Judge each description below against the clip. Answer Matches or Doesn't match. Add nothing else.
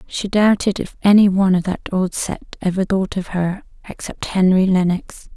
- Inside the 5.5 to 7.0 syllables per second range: Doesn't match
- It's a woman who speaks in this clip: Matches